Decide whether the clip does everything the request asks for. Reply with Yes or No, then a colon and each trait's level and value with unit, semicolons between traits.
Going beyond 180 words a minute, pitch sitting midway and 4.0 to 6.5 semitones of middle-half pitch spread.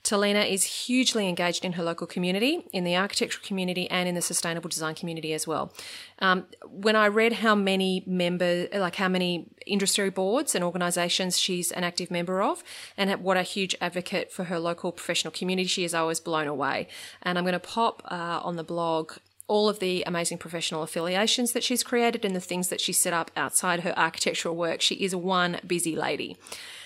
No: average, 200 wpm; medium, 180 Hz; narrow, 2.5 semitones